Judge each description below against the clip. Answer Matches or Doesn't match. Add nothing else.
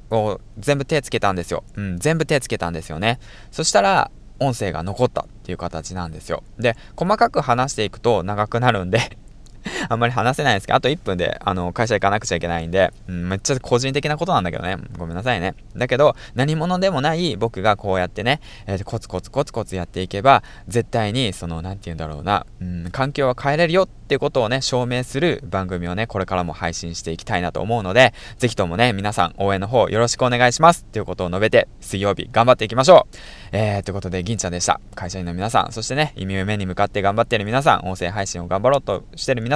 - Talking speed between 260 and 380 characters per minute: Doesn't match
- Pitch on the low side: Matches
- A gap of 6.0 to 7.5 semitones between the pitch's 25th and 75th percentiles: Doesn't match